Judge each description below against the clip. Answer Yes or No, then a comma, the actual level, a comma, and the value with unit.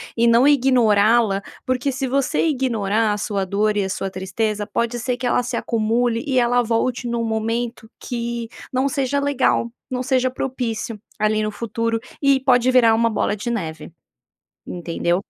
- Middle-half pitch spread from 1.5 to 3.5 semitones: Yes, average, 2.9 semitones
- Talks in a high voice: Yes, high, 235 Hz